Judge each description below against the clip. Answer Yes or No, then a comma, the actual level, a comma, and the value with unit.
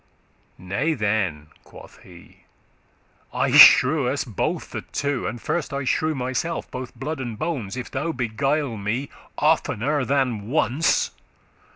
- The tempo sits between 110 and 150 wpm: Yes, average, 140 wpm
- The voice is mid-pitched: No, low, 130 Hz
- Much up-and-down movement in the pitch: No, average, 4.8 semitones